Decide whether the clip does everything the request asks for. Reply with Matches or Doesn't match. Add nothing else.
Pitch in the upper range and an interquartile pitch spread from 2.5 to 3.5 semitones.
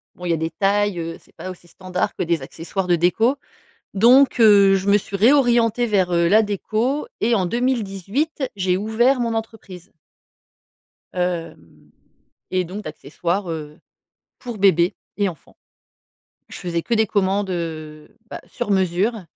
Doesn't match